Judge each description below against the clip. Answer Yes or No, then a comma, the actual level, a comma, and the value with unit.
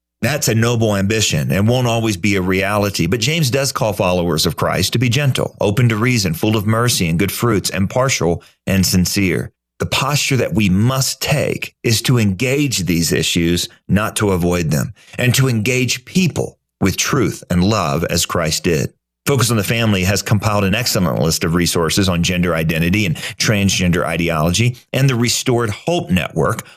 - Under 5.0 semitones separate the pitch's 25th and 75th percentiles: No, wide, 5.5 semitones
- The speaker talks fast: No, average, 180 wpm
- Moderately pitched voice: No, low, 110 Hz